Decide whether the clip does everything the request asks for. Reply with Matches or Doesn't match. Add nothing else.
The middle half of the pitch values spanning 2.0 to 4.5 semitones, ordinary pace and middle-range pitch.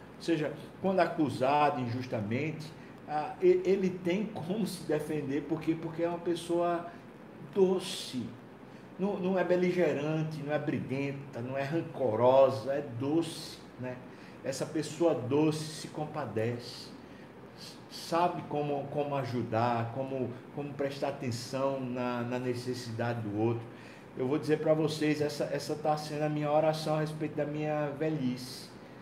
Matches